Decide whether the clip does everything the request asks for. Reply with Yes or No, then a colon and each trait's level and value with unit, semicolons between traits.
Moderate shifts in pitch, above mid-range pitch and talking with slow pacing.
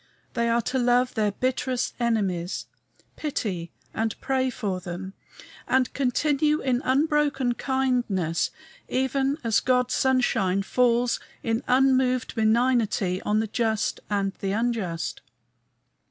Yes: average, 4.0 semitones; high, 240 Hz; slow, 115 wpm